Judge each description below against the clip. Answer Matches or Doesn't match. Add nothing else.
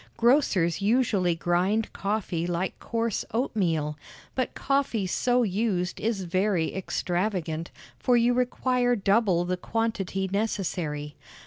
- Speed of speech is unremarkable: Doesn't match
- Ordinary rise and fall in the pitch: Matches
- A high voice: Matches